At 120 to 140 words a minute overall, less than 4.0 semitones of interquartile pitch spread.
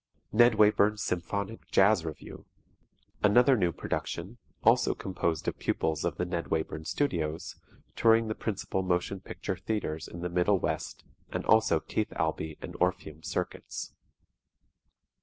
No: slow, 135 wpm; average, 4.4 semitones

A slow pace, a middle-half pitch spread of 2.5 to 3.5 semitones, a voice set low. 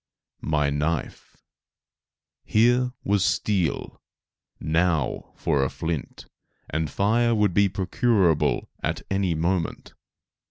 No: slow, 95 wpm; average, 4.6 semitones; very low, 90 Hz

